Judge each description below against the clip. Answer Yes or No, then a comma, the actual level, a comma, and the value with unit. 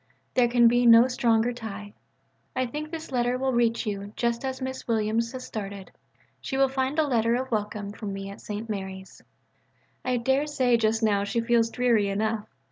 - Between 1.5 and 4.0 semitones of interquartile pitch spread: Yes, average, 3.2 semitones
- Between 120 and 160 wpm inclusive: No, average, 185 wpm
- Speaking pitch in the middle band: No, high, 235 Hz